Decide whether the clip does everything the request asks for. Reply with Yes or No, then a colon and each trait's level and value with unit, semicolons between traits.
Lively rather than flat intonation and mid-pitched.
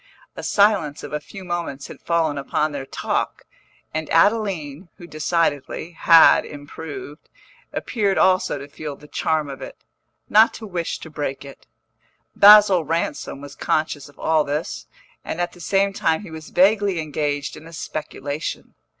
No: average, 3.7 semitones; medium, 160 Hz